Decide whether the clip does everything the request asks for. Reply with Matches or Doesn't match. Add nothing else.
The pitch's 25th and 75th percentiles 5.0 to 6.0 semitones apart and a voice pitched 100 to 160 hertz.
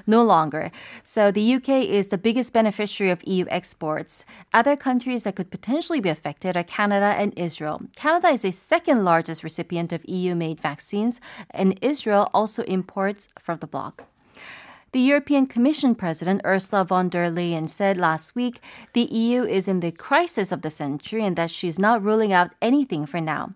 Doesn't match